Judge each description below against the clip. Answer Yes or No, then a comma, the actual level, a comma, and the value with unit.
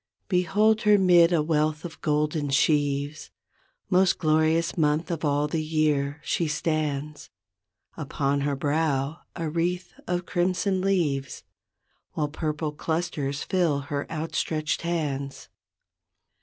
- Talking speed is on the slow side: Yes, slow, 115 wpm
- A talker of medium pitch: Yes, medium, 155 Hz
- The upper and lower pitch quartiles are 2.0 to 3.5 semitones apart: Yes, average, 2.8 semitones